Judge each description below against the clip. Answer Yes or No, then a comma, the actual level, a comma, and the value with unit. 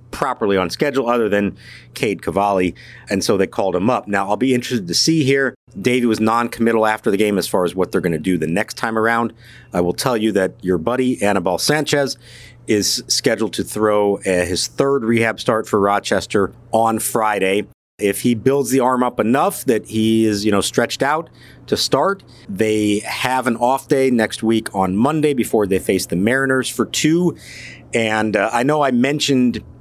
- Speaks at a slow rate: No, average, 195 wpm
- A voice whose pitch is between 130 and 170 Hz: No, low, 115 Hz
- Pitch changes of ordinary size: Yes, average, 3.8 semitones